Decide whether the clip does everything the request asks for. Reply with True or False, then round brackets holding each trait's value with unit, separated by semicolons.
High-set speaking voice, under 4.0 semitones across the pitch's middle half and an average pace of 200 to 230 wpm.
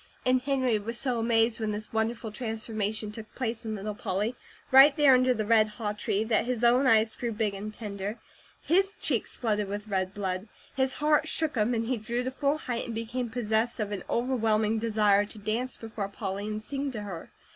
True (225 Hz; 2.9 semitones; 205 wpm)